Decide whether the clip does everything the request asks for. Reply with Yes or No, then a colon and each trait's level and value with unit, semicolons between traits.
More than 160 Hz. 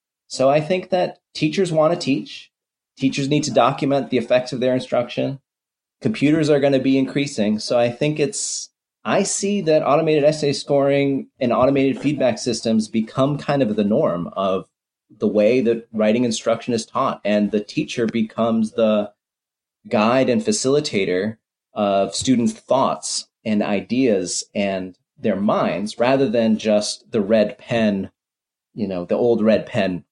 No: low, 125 Hz